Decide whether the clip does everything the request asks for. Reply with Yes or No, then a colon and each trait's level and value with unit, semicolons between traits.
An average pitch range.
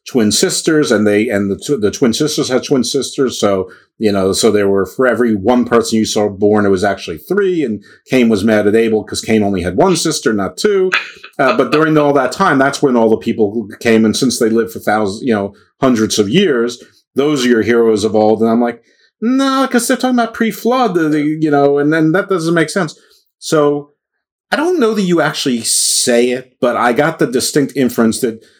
No: wide, 6.3 semitones